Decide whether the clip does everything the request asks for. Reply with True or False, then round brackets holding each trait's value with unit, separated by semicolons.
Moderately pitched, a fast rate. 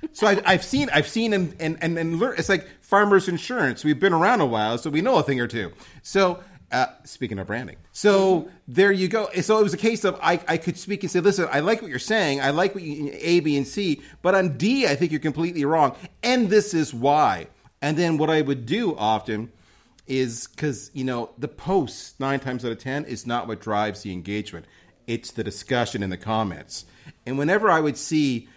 True (150 Hz; 225 wpm)